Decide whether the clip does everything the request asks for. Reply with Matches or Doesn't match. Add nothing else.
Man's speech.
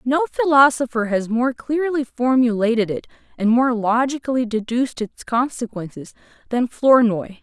Doesn't match